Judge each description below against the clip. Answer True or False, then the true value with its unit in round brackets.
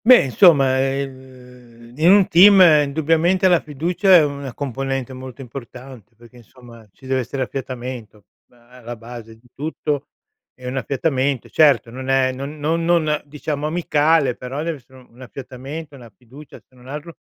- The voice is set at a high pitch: False (135 Hz)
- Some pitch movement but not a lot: True (3.4 semitones)